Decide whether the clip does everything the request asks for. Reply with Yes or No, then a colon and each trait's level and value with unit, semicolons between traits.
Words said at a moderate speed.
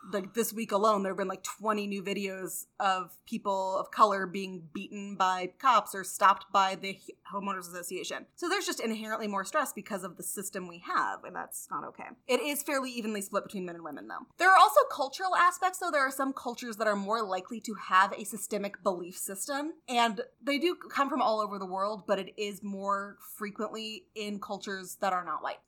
No: fast, 215 wpm